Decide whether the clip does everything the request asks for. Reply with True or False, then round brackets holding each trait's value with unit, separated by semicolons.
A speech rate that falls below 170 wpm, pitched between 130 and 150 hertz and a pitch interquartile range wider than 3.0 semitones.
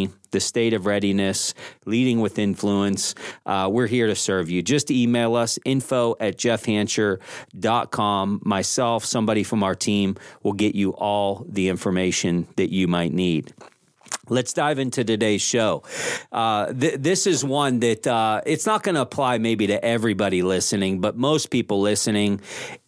False (155 wpm; 105 Hz; 3.4 semitones)